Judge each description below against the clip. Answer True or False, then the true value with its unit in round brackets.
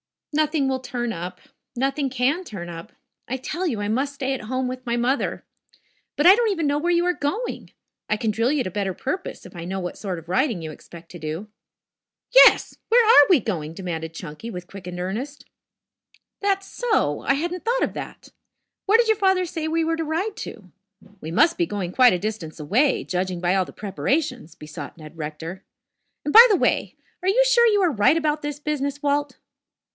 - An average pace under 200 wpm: False (205 wpm)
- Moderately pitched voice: False (260 Hz)